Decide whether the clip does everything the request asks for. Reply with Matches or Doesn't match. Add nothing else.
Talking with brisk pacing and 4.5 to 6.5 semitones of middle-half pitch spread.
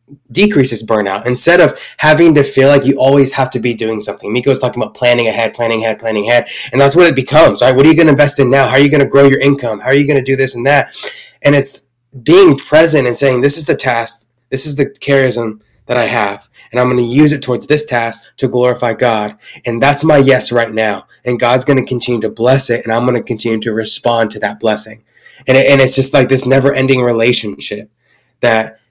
Doesn't match